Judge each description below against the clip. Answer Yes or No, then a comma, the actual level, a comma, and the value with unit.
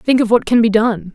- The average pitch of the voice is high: Yes, high, 220 Hz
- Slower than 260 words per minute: No, fast, 315 wpm